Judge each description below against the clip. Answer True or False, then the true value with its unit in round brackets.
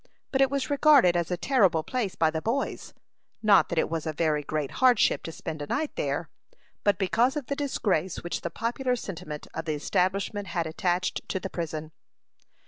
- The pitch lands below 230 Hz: True (185 Hz)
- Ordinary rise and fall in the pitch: False (7.5 semitones)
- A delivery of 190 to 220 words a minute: True (195 wpm)